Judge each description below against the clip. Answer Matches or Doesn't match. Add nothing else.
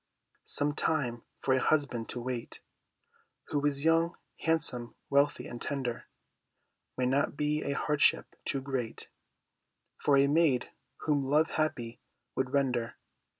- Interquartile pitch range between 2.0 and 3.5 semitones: Matches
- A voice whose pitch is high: Doesn't match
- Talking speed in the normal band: Doesn't match